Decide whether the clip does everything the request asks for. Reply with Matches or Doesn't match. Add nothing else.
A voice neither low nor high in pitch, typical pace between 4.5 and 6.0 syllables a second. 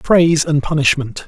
Matches